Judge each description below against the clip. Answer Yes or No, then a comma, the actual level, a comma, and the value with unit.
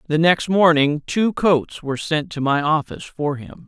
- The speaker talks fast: No, average, 195 wpm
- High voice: No, medium, 160 Hz